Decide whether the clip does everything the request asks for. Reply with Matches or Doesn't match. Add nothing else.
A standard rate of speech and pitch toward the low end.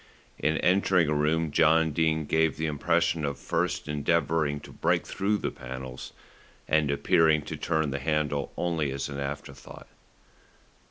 Matches